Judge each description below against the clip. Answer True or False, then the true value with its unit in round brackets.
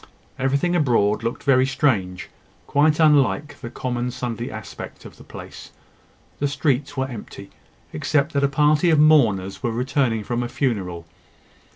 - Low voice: True (130 Hz)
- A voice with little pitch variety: False (4.1 semitones)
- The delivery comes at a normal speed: True (150 wpm)